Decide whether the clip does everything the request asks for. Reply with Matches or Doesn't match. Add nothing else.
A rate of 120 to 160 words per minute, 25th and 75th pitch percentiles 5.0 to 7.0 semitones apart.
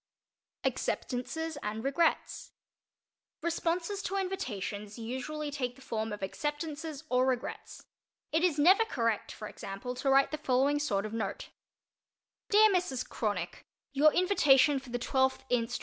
Matches